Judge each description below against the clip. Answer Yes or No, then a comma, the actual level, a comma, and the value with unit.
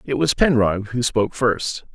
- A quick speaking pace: No, average, 185 wpm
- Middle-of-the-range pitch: No, low, 115 Hz